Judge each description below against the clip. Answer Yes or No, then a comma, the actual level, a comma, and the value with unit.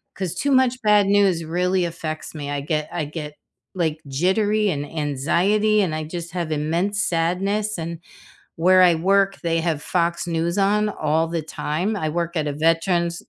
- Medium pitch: Yes, medium, 170 Hz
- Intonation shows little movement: No, average, 3.7 semitones